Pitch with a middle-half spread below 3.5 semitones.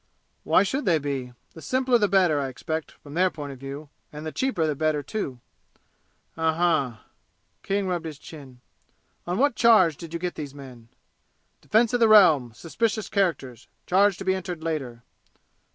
No: wide, 5.4 semitones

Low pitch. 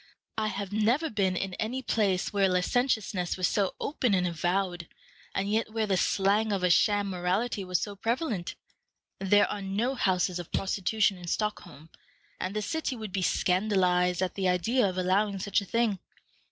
No: high, 195 Hz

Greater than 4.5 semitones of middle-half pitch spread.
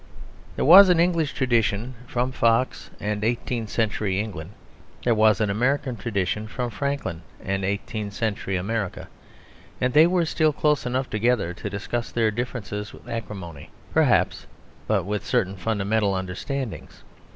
No: average, 4.0 semitones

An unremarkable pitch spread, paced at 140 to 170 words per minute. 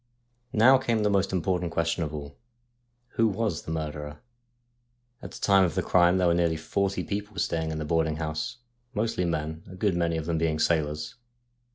No: average, 3.8 semitones; average, 190 wpm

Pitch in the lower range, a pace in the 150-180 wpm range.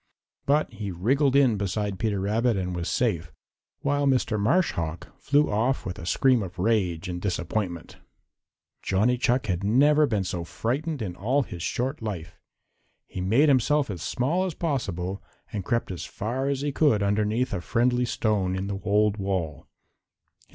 Yes: low, 105 Hz; average, 165 wpm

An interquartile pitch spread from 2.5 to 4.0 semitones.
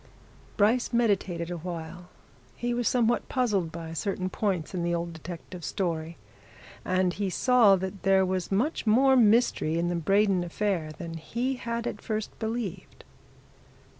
No: average, 4.7 semitones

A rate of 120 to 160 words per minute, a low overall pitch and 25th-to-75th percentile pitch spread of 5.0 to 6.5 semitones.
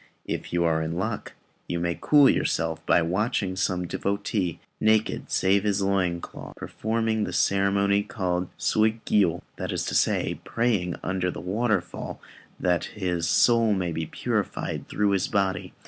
No: average, 150 wpm; very low, 95 Hz; average, 3.3 semitones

